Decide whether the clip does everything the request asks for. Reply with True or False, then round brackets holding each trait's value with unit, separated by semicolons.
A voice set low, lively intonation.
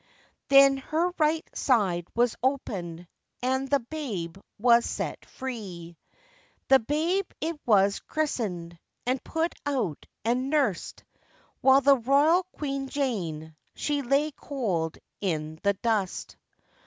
False (255 Hz; 6.8 semitones)